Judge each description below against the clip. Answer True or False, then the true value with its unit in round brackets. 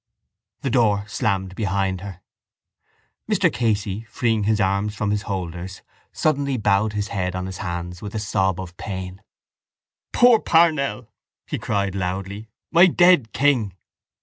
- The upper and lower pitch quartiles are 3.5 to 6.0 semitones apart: False (3.1 semitones)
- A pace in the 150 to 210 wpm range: False (140 wpm)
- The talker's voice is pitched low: True (100 Hz)